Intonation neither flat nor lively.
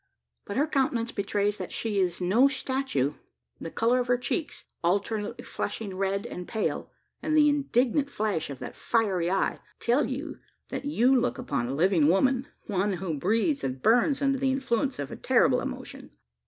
No: wide, 5.8 semitones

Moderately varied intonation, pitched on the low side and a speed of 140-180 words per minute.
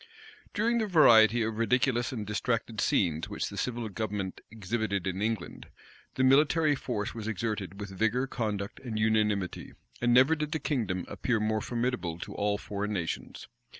Yes: average, 3.5 semitones; low, 110 Hz; average, 160 wpm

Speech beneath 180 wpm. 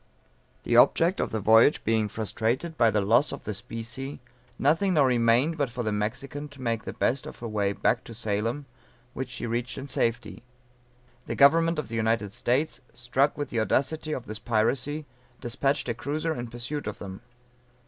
No: average, 190 wpm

